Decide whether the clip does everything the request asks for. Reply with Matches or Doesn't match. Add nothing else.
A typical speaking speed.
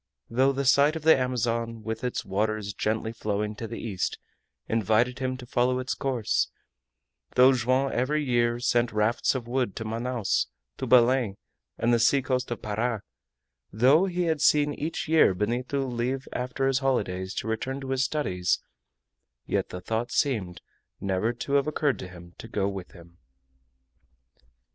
Matches